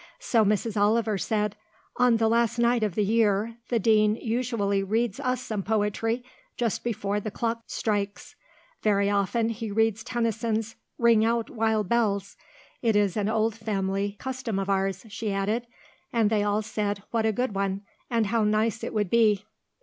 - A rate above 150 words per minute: Yes, average, 170 wpm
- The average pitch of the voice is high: Yes, high, 220 Hz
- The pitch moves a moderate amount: No, narrow, 2.1 semitones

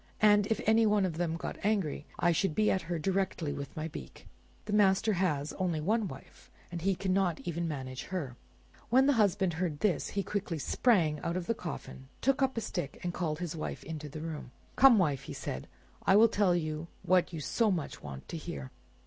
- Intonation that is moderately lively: Yes, average, 4.8 semitones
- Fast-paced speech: Yes, fast, 210 wpm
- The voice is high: No, medium, 175 Hz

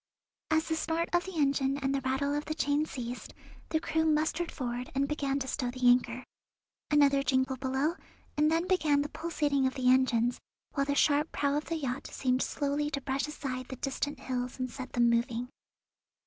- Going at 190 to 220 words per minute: Yes, average, 195 wpm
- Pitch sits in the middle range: No, very high, 275 Hz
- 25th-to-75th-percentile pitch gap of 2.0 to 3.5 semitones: Yes, average, 2.7 semitones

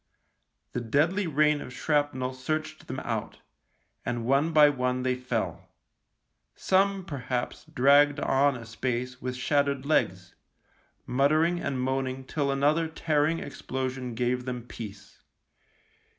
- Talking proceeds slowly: Yes, slow, 120 wpm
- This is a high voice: No, low, 135 Hz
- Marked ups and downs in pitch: No, average, 2.9 semitones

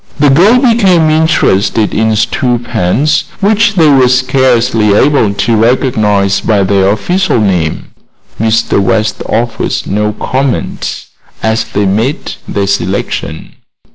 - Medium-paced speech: No, slow, 120 wpm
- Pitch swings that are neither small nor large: No, wide, 5.9 semitones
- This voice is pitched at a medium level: No, low, 115 Hz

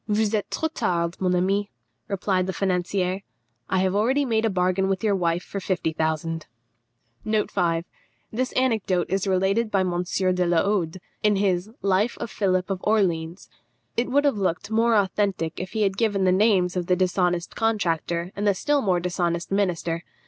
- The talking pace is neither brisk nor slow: Yes, average, 175 wpm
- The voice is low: No, high, 190 Hz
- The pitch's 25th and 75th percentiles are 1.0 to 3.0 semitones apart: Yes, average, 2.7 semitones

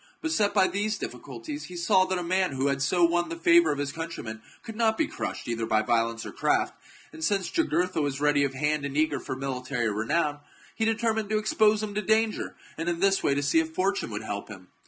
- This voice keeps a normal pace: No, fast, 240 wpm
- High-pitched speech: No, medium, 165 Hz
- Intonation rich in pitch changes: Yes, wide, 6.7 semitones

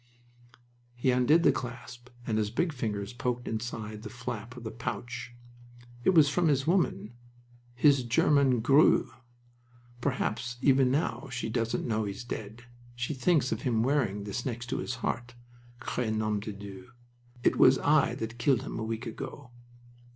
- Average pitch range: Yes, average, 3.2 semitones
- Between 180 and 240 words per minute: No, average, 160 wpm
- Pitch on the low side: Yes, low, 120 Hz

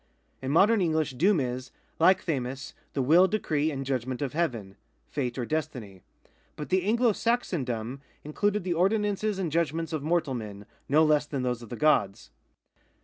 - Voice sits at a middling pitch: Yes, medium, 150 Hz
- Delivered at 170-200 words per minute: Yes, average, 175 wpm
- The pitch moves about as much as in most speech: No, wide, 5.9 semitones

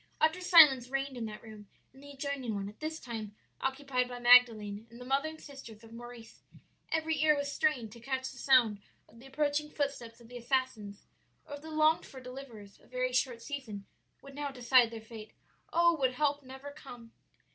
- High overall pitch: Yes, very high, 255 Hz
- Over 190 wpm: Yes, average, 200 wpm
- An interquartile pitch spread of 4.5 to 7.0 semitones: No, average, 3.7 semitones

